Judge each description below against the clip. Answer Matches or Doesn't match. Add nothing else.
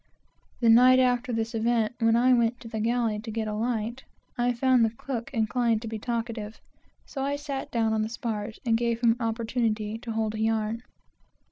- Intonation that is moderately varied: Doesn't match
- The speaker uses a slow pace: Doesn't match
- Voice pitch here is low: Doesn't match